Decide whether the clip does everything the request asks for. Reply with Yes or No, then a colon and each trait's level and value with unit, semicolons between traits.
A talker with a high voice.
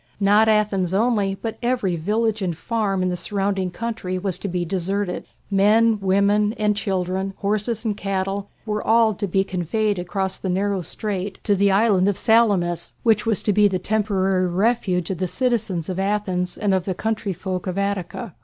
Yes: high, 200 Hz